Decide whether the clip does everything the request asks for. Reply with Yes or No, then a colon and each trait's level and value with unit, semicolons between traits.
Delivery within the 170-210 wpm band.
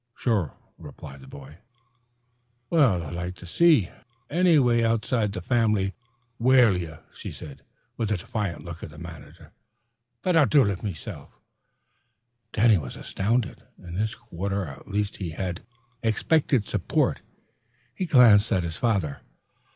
No: average, 145 wpm